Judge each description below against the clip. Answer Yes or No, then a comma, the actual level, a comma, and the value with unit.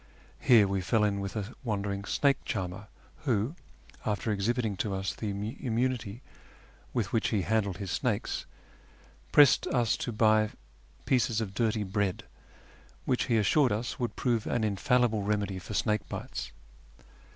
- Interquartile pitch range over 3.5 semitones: No, average, 3.0 semitones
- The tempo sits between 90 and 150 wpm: Yes, average, 145 wpm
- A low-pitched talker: Yes, low, 110 Hz